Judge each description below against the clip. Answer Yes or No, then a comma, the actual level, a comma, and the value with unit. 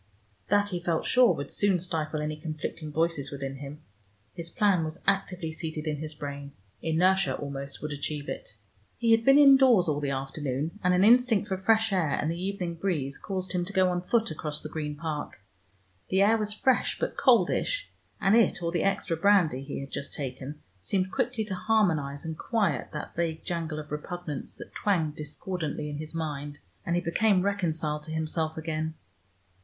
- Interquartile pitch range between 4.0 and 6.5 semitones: Yes, average, 4.4 semitones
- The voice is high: No, medium, 165 Hz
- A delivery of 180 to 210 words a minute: Yes, average, 185 wpm